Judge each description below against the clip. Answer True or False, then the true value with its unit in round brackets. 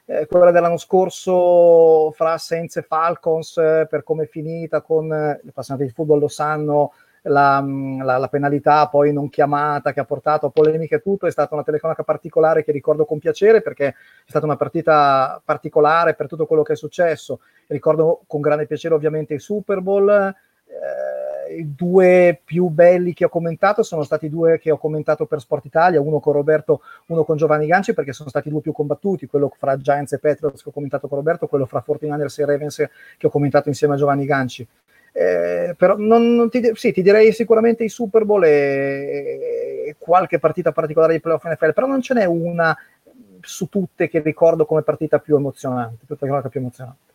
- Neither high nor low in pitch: True (155 Hz)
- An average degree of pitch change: True (3.0 semitones)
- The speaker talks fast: True (195 wpm)